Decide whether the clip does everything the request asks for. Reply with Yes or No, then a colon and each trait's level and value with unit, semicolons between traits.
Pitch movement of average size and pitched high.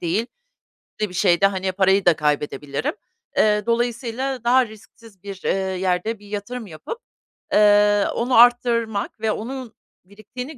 Yes: average, 3.6 semitones; high, 210 Hz